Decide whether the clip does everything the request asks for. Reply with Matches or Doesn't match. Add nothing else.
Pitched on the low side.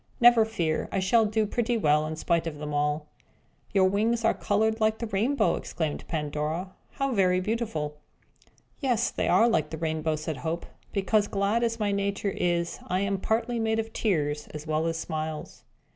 Doesn't match